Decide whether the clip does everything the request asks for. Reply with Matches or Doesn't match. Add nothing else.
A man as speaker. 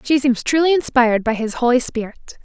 Doesn't match